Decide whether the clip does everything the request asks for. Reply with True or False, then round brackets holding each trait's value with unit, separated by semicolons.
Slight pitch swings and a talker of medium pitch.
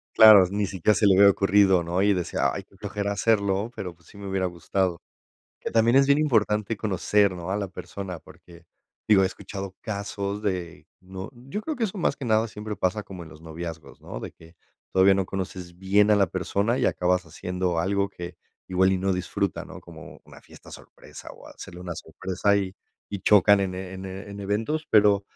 False (2.2 semitones; 95 Hz)